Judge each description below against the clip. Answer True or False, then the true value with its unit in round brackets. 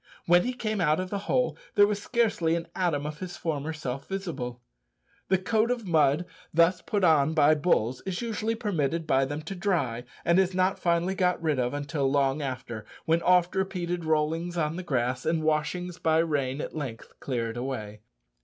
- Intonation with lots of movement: False (4.5 semitones)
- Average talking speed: True (190 wpm)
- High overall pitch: False (165 Hz)